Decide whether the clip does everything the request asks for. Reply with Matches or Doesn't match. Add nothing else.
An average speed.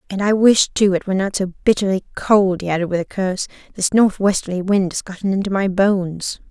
Doesn't match